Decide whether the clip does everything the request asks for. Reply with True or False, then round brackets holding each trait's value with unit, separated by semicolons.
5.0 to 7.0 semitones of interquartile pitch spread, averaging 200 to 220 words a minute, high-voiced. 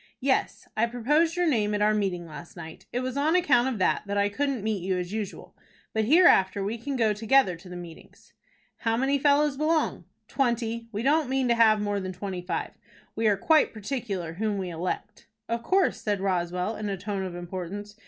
True (5.5 semitones; 205 wpm; 215 Hz)